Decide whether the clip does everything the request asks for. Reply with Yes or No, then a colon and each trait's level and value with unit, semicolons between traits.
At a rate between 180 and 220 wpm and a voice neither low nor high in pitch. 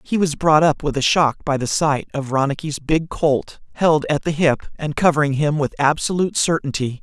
Yes: fast, 205 wpm; medium, 150 Hz